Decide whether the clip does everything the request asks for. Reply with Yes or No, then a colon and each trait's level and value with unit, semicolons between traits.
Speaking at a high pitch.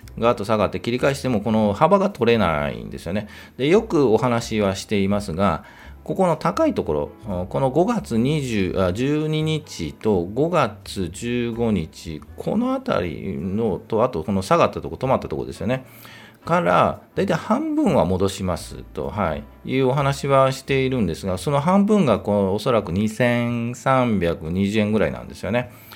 No: low, 115 Hz